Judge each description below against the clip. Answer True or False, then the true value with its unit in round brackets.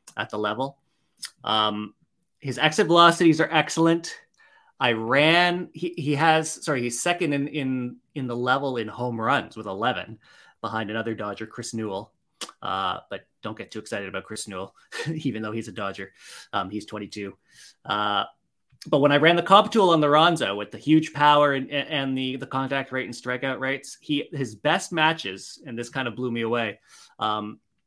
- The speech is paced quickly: False (185 wpm)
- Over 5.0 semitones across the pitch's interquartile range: True (5.6 semitones)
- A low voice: True (130 Hz)